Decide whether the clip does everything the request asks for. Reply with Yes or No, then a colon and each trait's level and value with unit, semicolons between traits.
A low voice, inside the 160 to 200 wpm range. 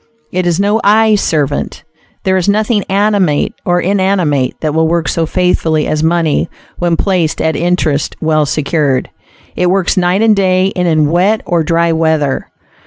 No: medium, 175 Hz; average, 165 wpm